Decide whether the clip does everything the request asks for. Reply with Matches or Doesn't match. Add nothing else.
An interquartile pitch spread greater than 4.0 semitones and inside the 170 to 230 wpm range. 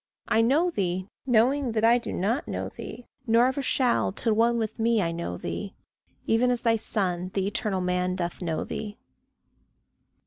Matches